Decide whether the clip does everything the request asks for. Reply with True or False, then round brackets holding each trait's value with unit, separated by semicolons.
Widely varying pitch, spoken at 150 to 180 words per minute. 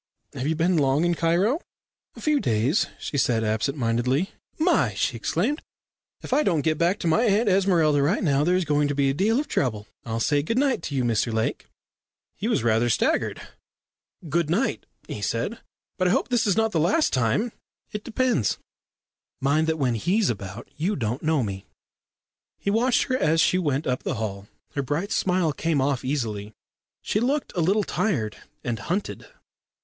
False (7.8 semitones; 190 wpm)